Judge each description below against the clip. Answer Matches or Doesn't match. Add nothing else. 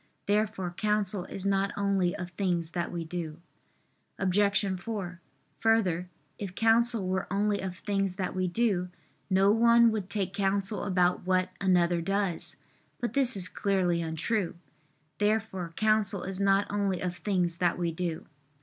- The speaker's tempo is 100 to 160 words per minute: Matches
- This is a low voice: Doesn't match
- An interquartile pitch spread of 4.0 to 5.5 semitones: Doesn't match